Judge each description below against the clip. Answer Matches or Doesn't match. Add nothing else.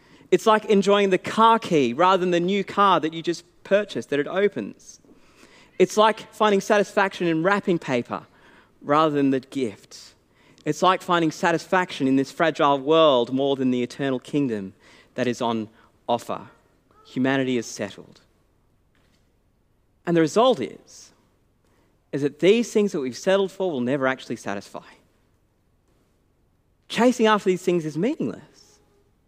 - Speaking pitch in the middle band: Matches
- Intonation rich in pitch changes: Matches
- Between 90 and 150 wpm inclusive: Matches